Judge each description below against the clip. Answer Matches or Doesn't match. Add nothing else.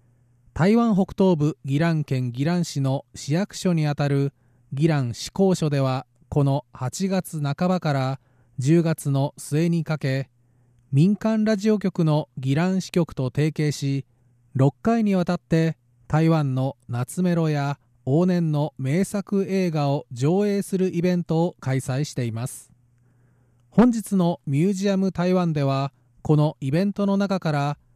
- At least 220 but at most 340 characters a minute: Matches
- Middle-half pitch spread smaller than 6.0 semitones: Matches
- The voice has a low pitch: Doesn't match